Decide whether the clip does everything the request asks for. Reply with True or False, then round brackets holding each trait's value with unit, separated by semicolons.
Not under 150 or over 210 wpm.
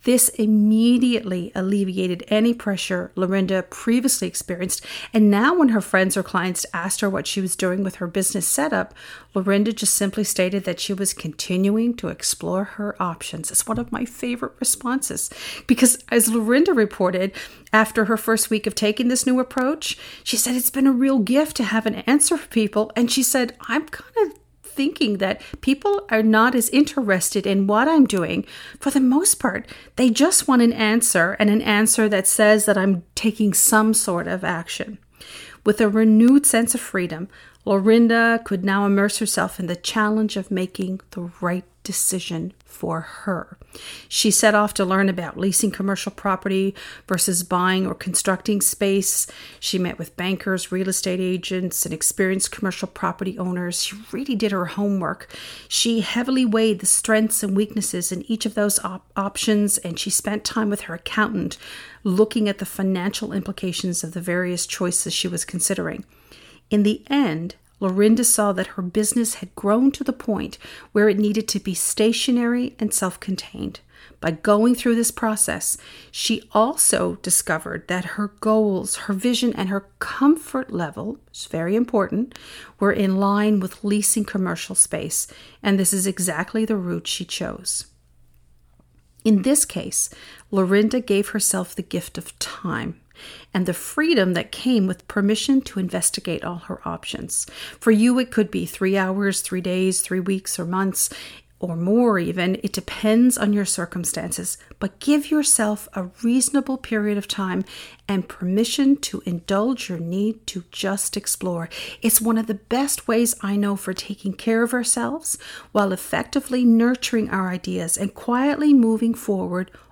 True (165 wpm)